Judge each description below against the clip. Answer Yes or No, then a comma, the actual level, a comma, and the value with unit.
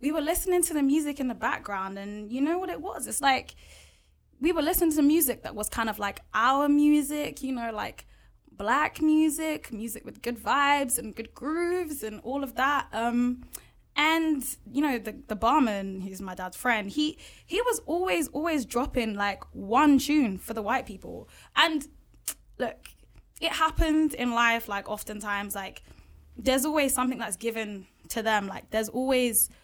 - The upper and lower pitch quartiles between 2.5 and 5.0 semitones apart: No, wide, 5.4 semitones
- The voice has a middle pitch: No, very high, 260 Hz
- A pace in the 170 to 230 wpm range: Yes, average, 180 wpm